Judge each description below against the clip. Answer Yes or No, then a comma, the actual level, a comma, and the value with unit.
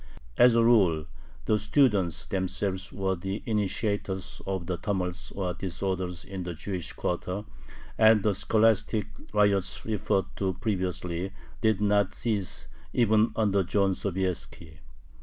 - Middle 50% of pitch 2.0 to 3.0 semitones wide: Yes, narrow, 2.5 semitones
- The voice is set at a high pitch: No, very low, 95 Hz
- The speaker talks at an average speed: No, slow, 125 wpm